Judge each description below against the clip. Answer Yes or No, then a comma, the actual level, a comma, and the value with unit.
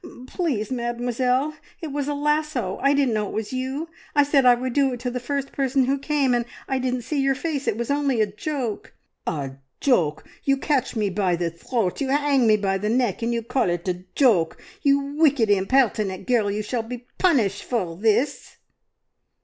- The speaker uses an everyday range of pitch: Yes, average, 4.6 semitones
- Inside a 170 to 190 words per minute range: No, fast, 205 wpm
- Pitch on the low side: No, very high, 250 Hz